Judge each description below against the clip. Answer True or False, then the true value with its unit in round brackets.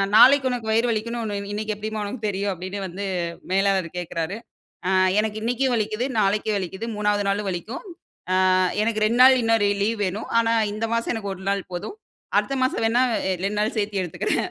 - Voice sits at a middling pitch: False (215 Hz)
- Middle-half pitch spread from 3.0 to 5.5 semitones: False (2.4 semitones)